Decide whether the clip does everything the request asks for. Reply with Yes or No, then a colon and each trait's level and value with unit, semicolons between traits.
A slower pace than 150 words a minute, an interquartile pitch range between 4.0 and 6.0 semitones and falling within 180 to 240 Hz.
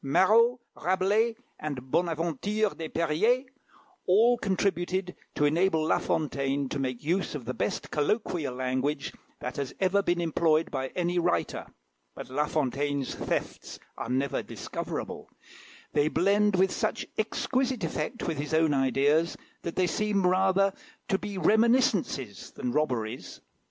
No: slow, 135 wpm; wide, 5.6 semitones; medium, 165 Hz